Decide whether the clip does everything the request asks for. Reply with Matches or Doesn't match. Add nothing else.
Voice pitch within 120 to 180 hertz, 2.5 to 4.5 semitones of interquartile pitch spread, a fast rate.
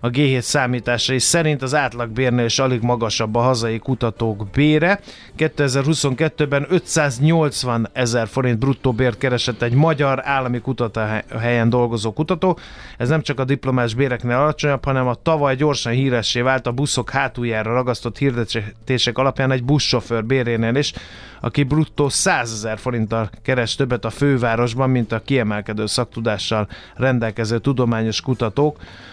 Doesn't match